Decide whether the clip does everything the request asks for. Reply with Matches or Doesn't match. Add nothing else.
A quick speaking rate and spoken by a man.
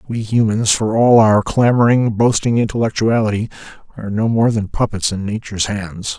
Doesn't match